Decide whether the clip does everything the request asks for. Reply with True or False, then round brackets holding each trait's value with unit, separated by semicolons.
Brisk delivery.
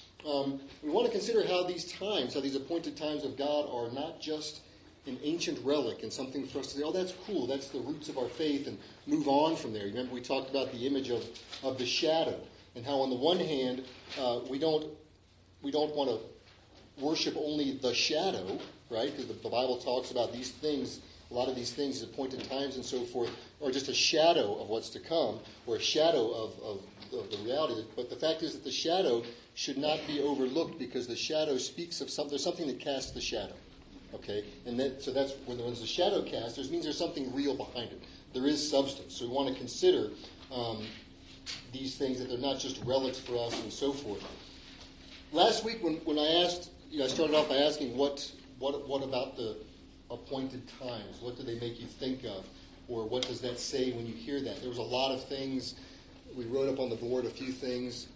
True (220 wpm)